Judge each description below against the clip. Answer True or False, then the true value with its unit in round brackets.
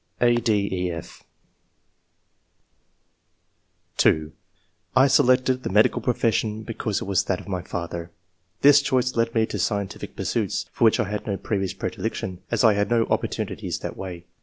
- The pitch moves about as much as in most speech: True (4.1 semitones)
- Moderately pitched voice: False (105 Hz)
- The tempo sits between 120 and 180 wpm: True (155 wpm)